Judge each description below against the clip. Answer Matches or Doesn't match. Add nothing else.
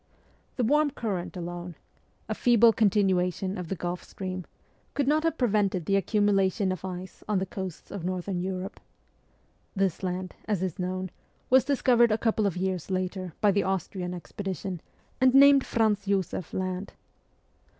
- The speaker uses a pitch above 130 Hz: Matches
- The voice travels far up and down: Doesn't match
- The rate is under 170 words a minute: Matches